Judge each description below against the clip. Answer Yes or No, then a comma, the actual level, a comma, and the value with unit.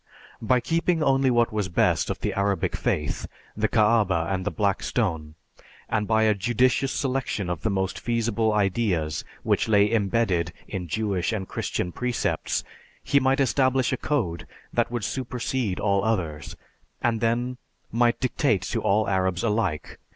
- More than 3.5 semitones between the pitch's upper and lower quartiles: Yes, average, 4.2 semitones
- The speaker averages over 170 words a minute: No, average, 155 wpm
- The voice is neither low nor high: No, low, 110 Hz